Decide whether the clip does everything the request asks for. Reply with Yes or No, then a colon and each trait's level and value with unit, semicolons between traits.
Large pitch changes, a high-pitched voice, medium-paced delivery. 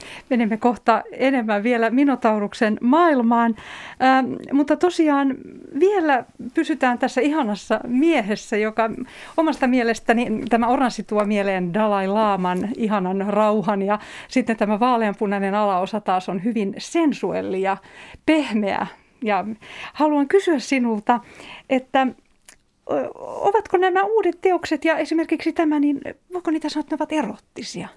Yes: wide, 6.1 semitones; high, 245 Hz; average, 120 wpm